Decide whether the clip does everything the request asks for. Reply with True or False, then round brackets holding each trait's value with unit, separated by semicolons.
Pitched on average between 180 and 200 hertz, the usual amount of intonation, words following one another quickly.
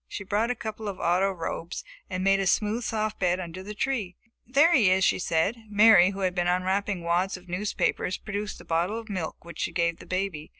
True (190 Hz; 3.0 semitones; 220 wpm)